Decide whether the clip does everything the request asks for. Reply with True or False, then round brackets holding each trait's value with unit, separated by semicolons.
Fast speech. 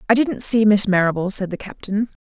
True (215 wpm)